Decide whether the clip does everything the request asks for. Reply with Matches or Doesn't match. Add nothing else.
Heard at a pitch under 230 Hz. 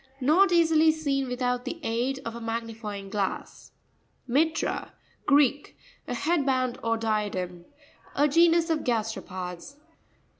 Doesn't match